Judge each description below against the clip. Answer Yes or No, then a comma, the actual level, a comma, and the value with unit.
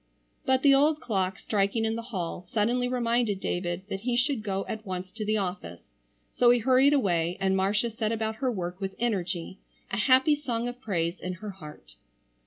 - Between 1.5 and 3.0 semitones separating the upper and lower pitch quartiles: No, average, 4.5 semitones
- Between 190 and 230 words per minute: Yes, average, 195 wpm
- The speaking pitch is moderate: No, high, 215 Hz